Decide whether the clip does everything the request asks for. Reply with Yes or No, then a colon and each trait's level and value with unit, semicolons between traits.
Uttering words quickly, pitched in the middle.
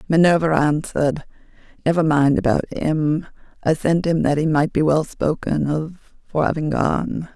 No: average, 155 wpm; medium, 155 Hz